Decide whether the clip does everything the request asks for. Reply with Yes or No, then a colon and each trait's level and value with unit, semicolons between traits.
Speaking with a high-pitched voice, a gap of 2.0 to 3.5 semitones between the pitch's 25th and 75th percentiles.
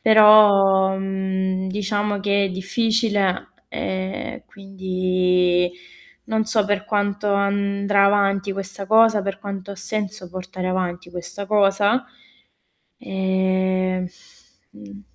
No: high, 195 Hz; narrow, 1.5 semitones